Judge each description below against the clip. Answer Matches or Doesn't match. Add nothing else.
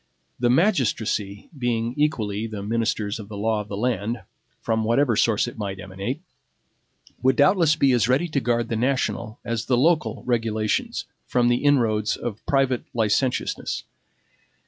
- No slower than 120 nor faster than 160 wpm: Matches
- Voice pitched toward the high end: Doesn't match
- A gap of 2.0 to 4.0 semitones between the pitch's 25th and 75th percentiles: Matches